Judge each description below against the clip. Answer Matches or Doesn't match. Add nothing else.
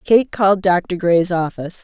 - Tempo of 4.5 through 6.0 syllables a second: Matches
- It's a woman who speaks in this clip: Matches